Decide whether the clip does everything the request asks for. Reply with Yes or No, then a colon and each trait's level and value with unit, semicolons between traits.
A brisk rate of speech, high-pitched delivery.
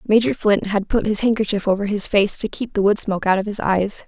Yes: fast, 265 wpm; high, 205 Hz